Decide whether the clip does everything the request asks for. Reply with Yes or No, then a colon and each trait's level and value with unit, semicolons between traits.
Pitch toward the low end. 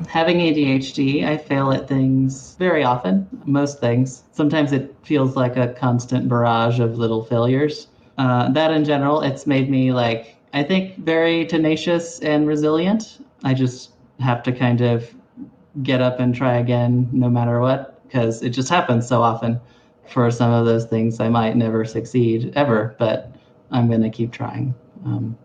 Yes: low, 125 Hz